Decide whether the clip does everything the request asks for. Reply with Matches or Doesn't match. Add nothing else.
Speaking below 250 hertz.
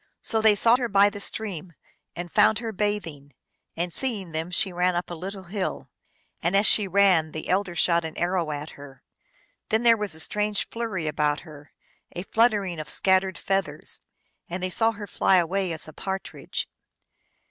Matches